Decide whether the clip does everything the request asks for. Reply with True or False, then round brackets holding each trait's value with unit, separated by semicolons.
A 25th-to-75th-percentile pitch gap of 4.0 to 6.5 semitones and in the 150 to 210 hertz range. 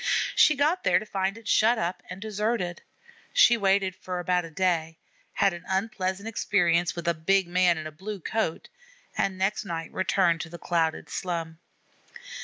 False (2.8 semitones; 185 Hz)